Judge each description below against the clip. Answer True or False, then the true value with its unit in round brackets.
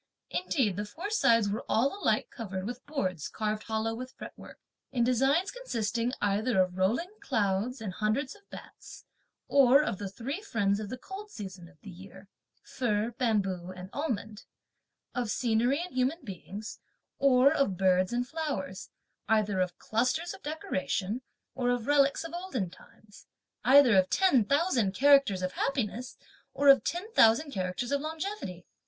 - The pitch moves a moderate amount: False (5.8 semitones)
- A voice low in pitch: False (235 Hz)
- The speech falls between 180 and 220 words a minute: False (160 wpm)